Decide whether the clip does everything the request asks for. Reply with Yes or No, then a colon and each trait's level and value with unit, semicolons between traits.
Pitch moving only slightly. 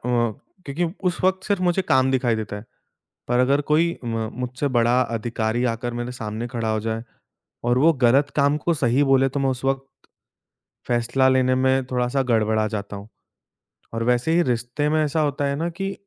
No: average, 3.4 semitones